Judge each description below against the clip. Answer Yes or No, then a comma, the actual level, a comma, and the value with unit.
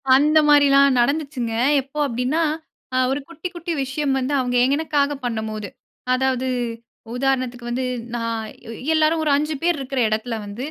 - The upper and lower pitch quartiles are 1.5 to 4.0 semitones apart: Yes, average, 3.3 semitones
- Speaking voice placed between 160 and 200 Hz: No, very high, 265 Hz